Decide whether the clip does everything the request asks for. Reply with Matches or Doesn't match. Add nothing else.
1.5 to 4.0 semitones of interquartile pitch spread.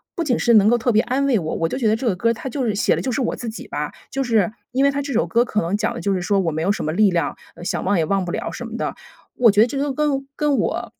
Doesn't match